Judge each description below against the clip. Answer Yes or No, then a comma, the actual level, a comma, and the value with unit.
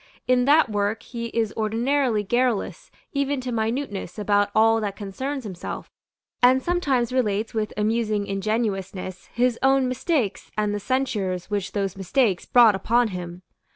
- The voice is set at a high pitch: Yes, high, 220 Hz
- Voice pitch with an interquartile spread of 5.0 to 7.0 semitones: No, average, 3.8 semitones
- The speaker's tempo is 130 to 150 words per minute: Yes, average, 145 wpm